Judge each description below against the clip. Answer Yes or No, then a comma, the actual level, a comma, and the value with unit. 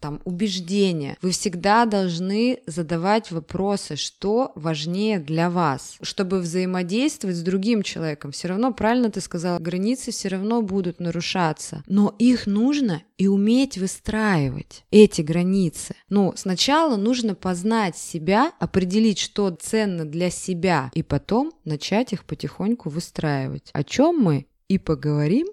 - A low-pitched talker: No, high, 190 Hz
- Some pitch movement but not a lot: Yes, average, 4.4 semitones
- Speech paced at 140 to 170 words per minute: No, average, 130 wpm